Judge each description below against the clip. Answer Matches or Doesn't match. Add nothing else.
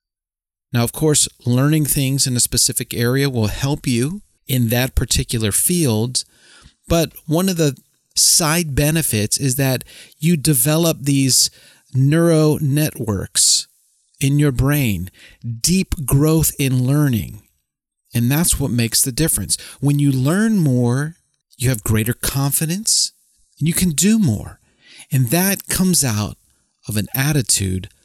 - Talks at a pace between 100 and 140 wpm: Matches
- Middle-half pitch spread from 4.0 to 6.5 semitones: Matches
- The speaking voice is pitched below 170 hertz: Matches